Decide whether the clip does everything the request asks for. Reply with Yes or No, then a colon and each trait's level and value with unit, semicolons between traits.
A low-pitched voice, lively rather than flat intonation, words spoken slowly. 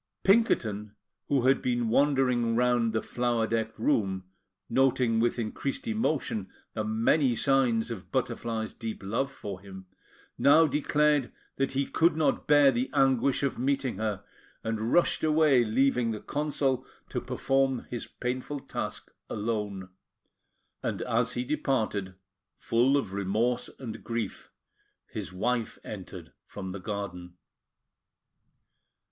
No: low, 120 Hz; average, 3.7 semitones; slow, 130 wpm